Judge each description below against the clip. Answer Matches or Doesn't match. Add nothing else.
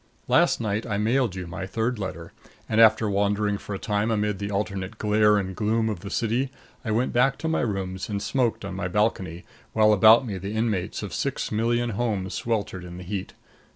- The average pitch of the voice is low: Matches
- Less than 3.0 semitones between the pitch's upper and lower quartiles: Matches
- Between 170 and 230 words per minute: Matches